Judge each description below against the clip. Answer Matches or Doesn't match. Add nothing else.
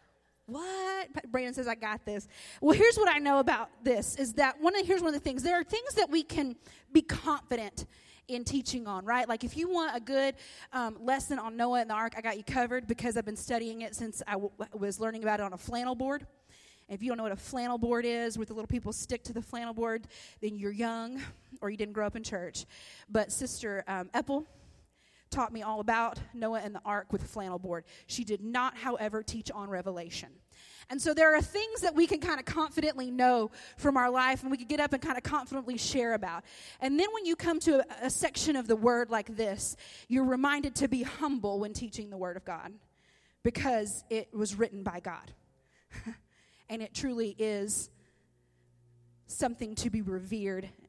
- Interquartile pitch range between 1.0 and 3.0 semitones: Doesn't match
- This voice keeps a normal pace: Doesn't match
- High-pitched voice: Matches